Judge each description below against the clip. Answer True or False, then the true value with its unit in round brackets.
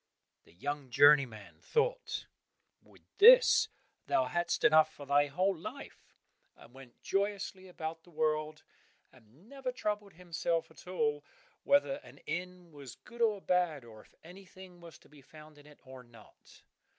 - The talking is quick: False (150 wpm)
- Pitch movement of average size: True (4.7 semitones)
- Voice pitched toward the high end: False (160 Hz)